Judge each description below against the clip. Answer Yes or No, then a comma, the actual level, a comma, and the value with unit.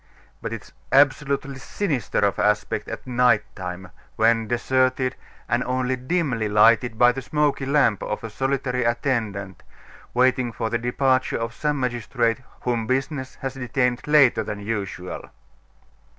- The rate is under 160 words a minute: Yes, average, 140 wpm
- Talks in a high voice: No, low, 125 Hz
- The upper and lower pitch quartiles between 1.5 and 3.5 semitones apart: Yes, average, 2.8 semitones